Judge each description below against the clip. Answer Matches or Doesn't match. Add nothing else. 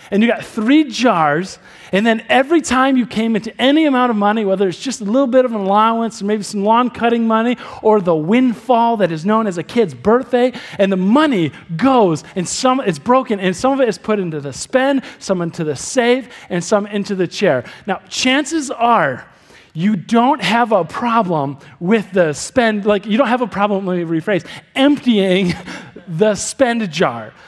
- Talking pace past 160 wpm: Matches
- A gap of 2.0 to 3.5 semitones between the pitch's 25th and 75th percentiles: Doesn't match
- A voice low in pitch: Doesn't match